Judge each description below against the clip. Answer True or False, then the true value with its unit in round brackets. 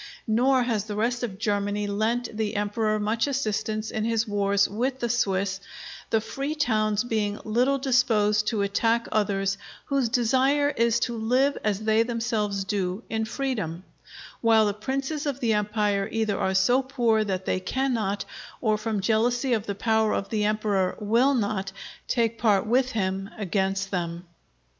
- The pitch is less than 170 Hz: False (220 Hz)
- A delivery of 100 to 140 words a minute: False (160 wpm)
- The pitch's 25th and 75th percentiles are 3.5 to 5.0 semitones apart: False (2.8 semitones)